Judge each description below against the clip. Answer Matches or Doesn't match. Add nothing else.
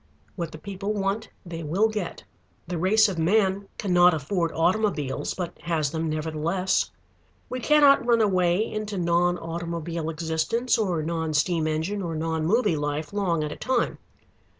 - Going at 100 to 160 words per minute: Matches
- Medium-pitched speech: Matches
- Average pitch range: Matches